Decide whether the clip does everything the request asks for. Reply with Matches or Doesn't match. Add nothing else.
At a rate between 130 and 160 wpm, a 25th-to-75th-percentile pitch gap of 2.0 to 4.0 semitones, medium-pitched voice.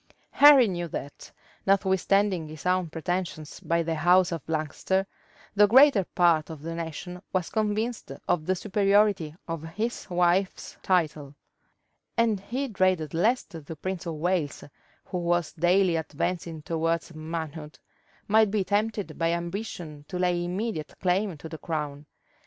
Matches